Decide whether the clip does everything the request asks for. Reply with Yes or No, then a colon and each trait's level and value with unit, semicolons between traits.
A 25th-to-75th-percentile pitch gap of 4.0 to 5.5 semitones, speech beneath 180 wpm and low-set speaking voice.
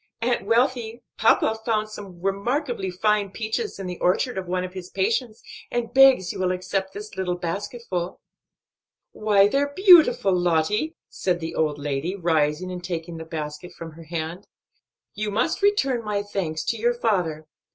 No: average, 4.7 semitones; average, 165 wpm; high, 195 Hz